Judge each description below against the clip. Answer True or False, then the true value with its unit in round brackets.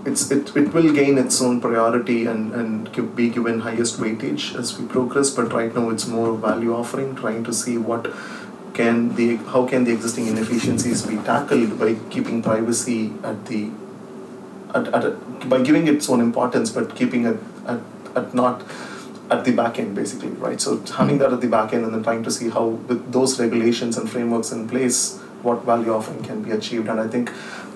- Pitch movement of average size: False (1.5 semitones)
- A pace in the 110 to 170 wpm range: False (195 wpm)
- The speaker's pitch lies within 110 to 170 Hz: True (120 Hz)